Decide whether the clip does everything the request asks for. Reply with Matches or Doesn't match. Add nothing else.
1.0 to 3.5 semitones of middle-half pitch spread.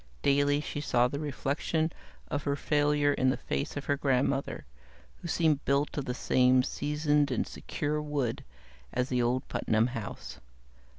Matches